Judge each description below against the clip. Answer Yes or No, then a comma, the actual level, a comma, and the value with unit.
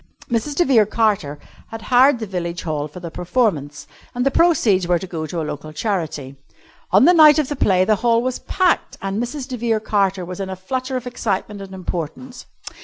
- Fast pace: Yes, fast, 210 wpm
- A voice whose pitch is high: Yes, high, 205 Hz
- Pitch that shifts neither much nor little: No, wide, 6.0 semitones